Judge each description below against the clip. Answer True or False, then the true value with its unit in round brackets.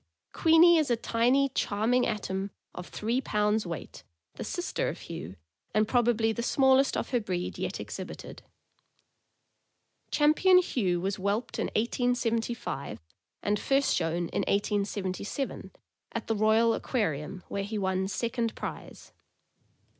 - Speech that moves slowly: True (130 wpm)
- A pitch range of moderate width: True (4.1 semitones)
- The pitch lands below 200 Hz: False (220 Hz)